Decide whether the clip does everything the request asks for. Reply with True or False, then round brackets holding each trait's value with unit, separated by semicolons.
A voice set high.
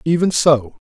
False (150 Hz)